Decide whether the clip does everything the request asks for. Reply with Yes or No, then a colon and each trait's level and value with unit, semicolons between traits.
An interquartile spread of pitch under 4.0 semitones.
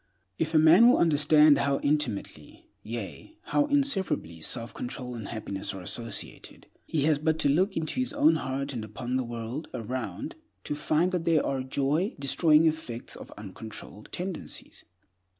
No: wide, 5.5 semitones